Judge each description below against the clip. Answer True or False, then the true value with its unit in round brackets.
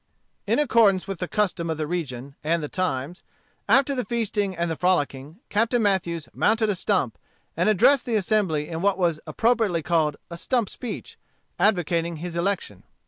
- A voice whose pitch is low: False (180 Hz)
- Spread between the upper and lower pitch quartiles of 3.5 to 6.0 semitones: True (4.6 semitones)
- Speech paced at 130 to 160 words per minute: False (170 wpm)